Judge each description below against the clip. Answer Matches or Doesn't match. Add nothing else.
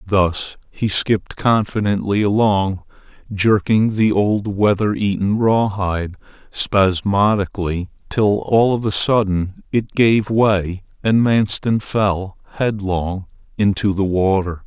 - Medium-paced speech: Doesn't match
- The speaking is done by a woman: Doesn't match